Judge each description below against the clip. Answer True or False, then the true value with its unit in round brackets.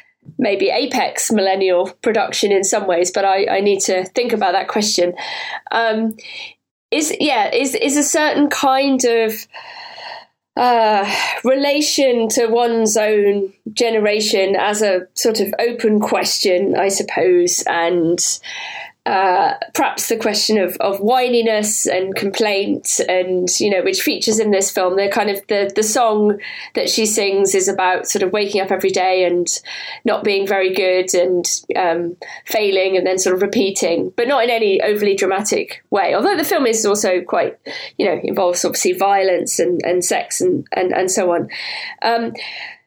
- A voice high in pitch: True (205 Hz)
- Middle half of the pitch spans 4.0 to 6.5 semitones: False (3.3 semitones)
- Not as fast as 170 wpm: True (160 wpm)